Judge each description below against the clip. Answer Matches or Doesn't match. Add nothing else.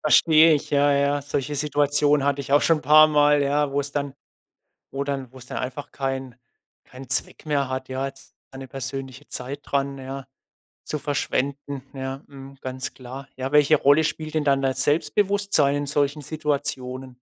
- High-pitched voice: Doesn't match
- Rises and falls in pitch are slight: Matches